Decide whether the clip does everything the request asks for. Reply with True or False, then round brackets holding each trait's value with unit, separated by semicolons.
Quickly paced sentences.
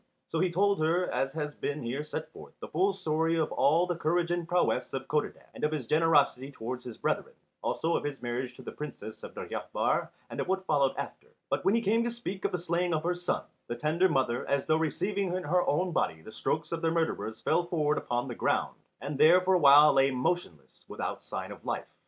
True (230 wpm)